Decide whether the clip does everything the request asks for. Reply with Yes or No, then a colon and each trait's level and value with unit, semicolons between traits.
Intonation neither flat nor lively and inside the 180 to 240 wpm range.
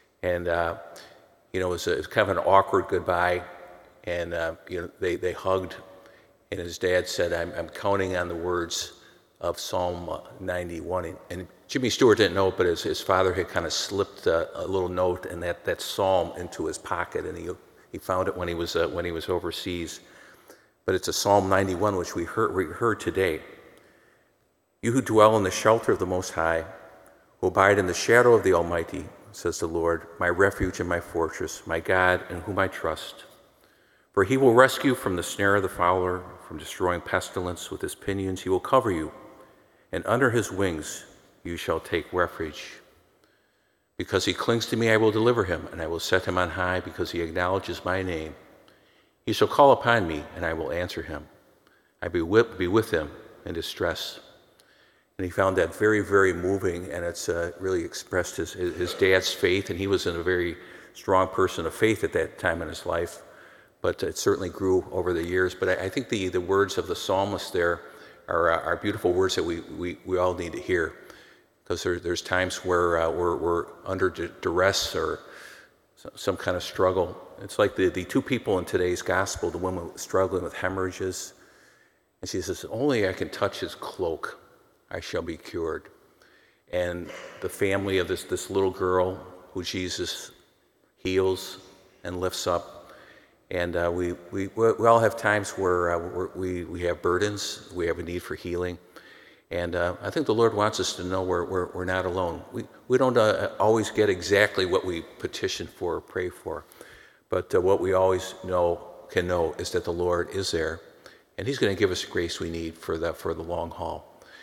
No: narrow, 2.0 semitones; average, 200 wpm